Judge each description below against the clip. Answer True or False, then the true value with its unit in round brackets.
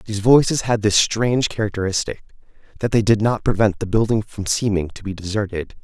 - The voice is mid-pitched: False (105 Hz)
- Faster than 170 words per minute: True (185 wpm)